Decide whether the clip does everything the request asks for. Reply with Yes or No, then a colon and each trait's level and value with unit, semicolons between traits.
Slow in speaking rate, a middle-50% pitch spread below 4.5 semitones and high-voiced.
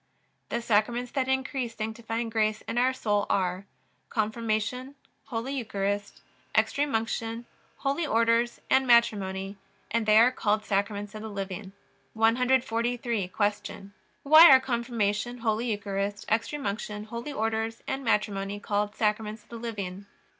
Yes: slow, 130 wpm; narrow, 2.6 semitones; high, 225 Hz